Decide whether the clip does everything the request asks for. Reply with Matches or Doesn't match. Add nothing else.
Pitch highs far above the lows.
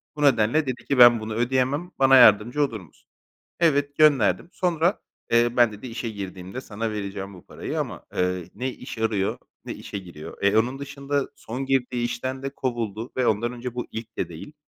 Doesn't match